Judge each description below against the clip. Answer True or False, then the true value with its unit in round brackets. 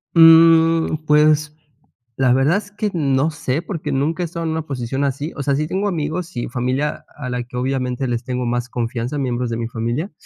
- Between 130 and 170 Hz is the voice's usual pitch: True (140 Hz)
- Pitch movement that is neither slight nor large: True (4.4 semitones)